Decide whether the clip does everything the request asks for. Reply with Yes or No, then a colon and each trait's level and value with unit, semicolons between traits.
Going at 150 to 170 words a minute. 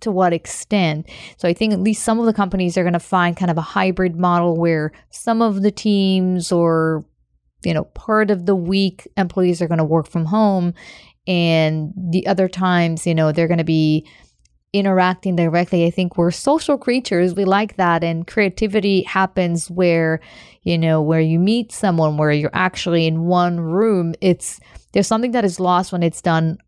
No: average, 190 wpm